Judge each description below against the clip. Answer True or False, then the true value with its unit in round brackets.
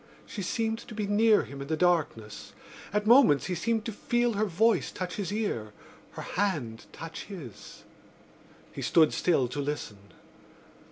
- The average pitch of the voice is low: False (180 Hz)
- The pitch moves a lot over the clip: True (6.9 semitones)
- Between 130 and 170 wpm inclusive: True (160 wpm)